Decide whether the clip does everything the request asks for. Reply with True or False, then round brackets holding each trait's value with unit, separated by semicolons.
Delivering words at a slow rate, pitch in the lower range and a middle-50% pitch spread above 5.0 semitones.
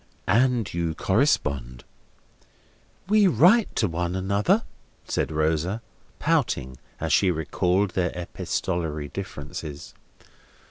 True (95 wpm; 90 Hz; 5.6 semitones)